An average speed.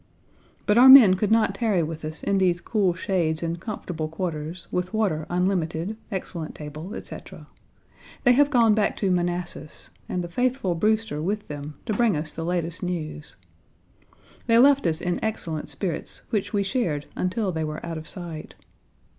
Yes: average, 170 wpm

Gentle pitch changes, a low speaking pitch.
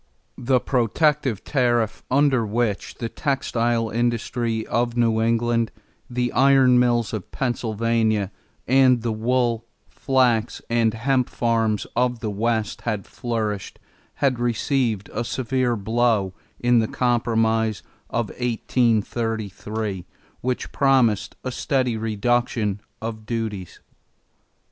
Yes: narrow, 1.9 semitones; low, 115 Hz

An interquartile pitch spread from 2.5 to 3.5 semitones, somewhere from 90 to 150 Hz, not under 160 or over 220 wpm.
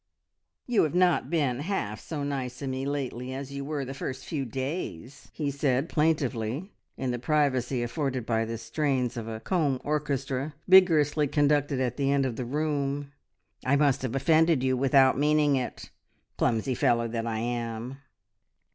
Yes: average, 2.9 semitones; low, 135 Hz; average, 165 wpm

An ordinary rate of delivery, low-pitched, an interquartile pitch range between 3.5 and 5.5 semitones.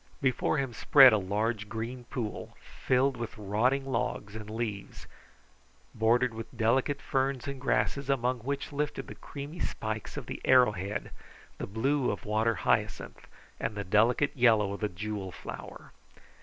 Yes: average, 155 wpm; low, 115 Hz; average, 3.8 semitones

